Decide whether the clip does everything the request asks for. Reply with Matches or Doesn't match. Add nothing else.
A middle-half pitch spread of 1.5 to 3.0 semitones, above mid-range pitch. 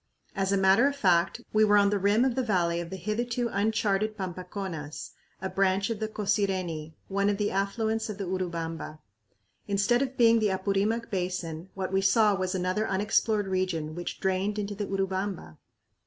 Matches